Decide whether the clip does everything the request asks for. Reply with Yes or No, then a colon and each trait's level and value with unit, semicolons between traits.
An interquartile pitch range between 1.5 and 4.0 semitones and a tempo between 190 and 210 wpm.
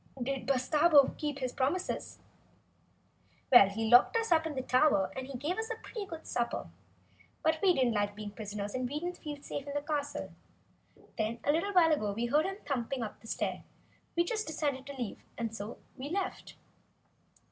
No: average, 5.1 semitones; average, 200 wpm